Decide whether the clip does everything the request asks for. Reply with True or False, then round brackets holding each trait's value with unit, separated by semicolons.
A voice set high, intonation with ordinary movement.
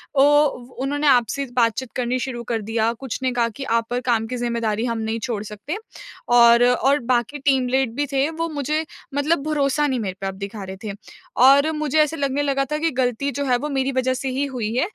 True (255 Hz; 3.3 semitones)